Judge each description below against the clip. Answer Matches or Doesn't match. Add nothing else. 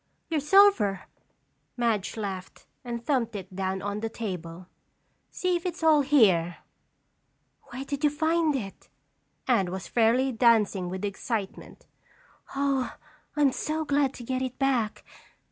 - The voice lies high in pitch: Matches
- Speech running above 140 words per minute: Doesn't match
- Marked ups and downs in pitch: Matches